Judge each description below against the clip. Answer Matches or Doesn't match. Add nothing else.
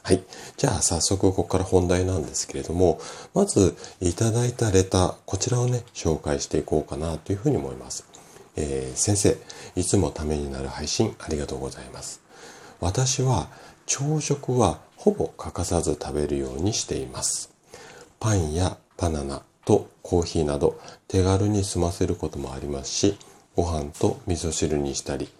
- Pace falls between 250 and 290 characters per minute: Doesn't match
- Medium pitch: Doesn't match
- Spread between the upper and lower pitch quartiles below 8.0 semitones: Matches